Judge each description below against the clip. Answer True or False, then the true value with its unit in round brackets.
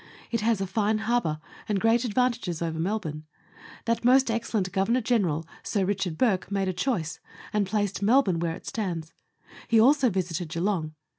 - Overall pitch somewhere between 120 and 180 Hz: False (200 Hz)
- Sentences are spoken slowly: False (165 wpm)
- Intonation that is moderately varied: True (4.8 semitones)